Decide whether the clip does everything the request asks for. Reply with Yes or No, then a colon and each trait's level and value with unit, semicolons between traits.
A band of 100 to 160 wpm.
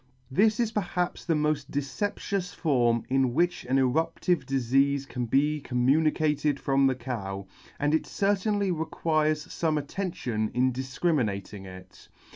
Yes: slow, 135 wpm